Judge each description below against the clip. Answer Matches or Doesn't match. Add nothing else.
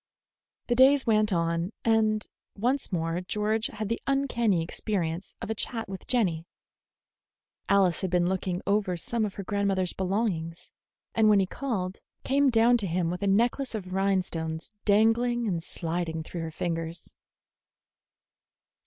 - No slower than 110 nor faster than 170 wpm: Matches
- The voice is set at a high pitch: Matches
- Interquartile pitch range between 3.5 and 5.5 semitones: Matches